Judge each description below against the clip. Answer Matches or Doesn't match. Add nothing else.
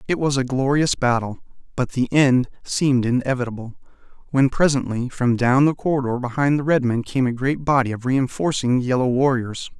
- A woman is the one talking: Doesn't match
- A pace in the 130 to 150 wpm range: Doesn't match